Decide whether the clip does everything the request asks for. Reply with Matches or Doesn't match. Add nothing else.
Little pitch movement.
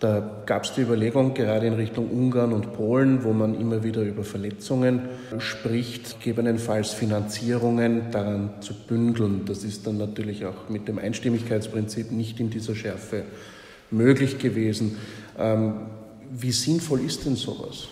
Matches